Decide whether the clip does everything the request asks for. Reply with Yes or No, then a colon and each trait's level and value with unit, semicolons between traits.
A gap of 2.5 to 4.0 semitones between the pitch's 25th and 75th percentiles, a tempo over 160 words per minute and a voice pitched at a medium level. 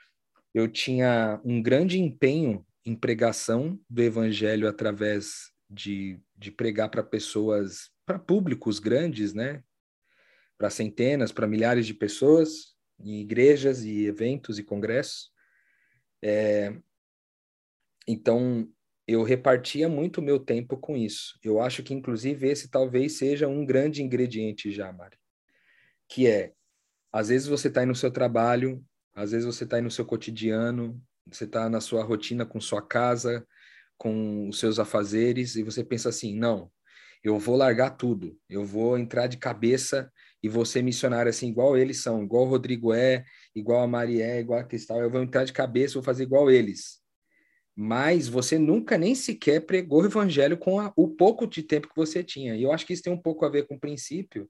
No: average, 3.6 semitones; average, 170 wpm; low, 120 Hz